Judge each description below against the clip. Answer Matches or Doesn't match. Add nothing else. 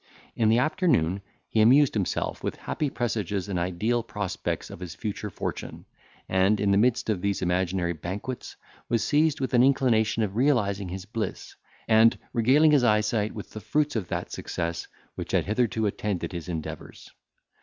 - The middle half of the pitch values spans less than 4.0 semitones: Doesn't match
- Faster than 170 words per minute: Doesn't match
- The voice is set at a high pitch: Doesn't match